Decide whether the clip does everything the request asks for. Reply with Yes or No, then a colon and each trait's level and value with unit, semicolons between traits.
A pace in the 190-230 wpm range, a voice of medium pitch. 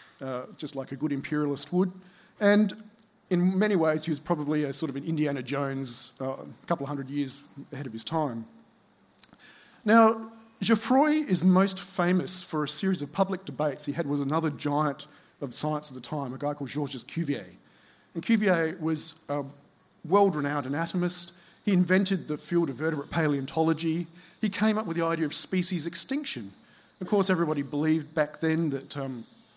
No: average, 175 wpm; medium, 160 Hz